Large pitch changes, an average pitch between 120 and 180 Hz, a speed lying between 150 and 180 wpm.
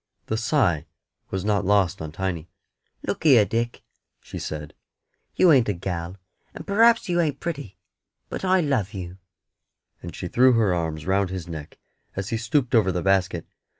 No: wide, 6.1 semitones; low, 100 Hz; average, 170 wpm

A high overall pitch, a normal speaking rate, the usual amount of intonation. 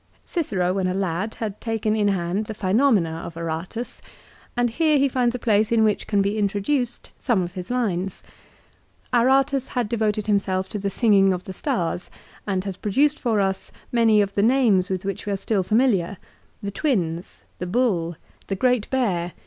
Yes: high, 205 Hz; average, 190 wpm; average, 4.2 semitones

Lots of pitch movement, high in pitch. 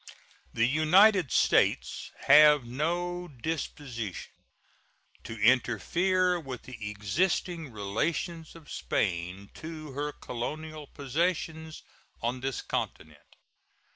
No: wide, 5.9 semitones; medium, 150 Hz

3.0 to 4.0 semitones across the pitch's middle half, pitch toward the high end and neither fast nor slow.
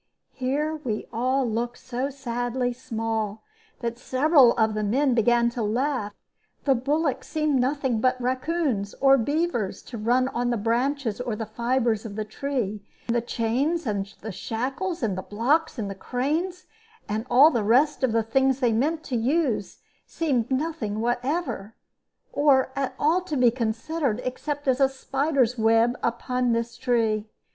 Yes: average, 3.6 semitones; high, 245 Hz; average, 160 wpm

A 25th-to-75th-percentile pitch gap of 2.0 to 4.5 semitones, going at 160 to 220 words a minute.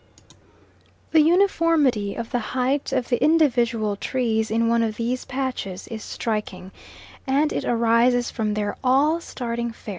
No: average, 3.3 semitones; average, 145 wpm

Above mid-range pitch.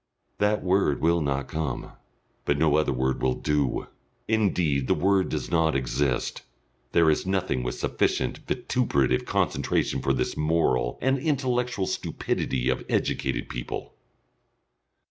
No: very low, 75 Hz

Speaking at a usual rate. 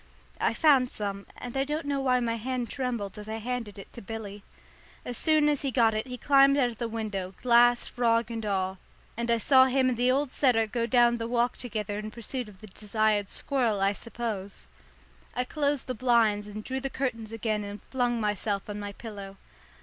No: fast, 210 wpm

